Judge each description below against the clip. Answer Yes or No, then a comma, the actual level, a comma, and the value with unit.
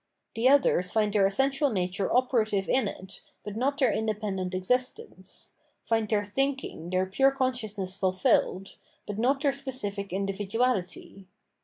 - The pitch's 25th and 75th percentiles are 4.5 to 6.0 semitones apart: Yes, average, 5.0 semitones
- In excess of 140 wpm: No, slow, 135 wpm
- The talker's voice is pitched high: Yes, high, 210 Hz